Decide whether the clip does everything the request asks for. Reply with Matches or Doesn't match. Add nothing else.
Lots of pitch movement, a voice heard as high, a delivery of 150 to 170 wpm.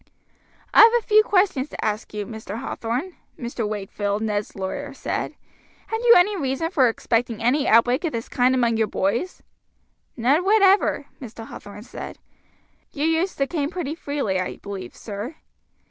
Matches